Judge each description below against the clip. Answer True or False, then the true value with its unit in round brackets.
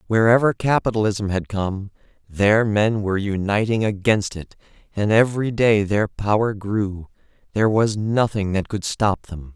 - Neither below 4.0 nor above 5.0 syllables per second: True (4.6 syllables/s)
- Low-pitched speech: True (105 Hz)